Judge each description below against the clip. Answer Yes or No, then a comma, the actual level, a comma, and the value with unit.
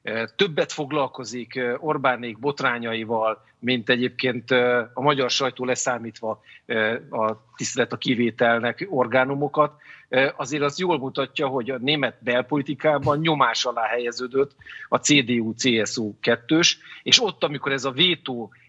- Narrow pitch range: No, average, 3.6 semitones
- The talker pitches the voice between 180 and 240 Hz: No, low, 125 Hz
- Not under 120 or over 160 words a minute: No, average, 110 wpm